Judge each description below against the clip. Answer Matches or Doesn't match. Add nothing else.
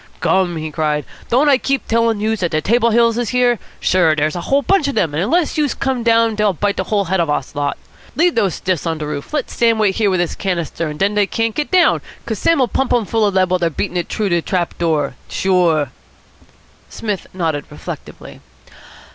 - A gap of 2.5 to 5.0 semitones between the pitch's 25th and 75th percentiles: Doesn't match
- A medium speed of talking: Doesn't match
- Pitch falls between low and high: Doesn't match